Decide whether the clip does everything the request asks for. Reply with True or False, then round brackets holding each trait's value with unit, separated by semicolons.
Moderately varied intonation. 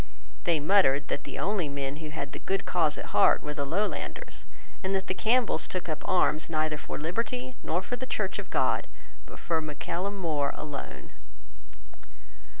True (4.5 semitones)